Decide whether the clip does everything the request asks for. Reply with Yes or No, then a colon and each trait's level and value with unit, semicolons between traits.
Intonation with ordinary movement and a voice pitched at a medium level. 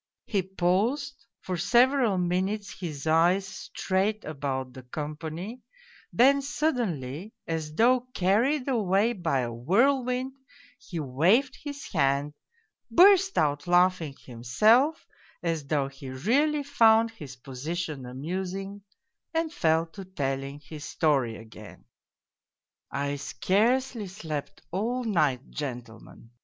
No: wide, 8.4 semitones; medium, 180 Hz